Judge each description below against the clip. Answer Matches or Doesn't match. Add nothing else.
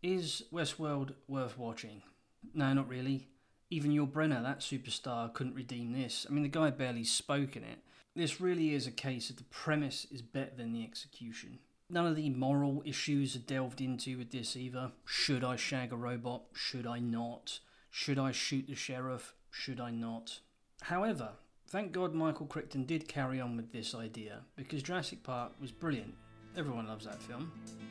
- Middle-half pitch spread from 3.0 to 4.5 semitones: Matches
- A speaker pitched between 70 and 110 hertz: Doesn't match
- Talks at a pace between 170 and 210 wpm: Matches